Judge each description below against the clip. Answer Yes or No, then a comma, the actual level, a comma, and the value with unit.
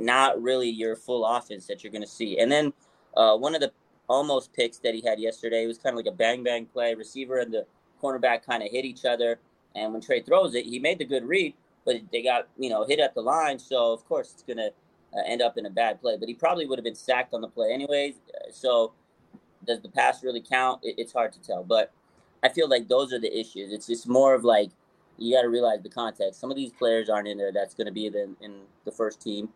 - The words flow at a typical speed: No, fast, 250 wpm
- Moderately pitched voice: No, low, 120 Hz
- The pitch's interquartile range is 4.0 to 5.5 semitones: No, average, 2.9 semitones